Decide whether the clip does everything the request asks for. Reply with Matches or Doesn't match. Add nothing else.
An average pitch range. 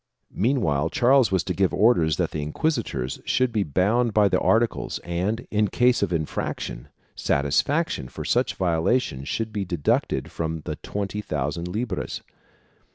Doesn't match